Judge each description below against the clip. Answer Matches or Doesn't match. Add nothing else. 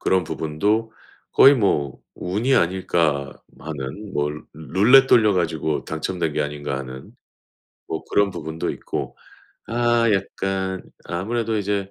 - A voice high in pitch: Doesn't match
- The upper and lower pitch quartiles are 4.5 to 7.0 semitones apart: Matches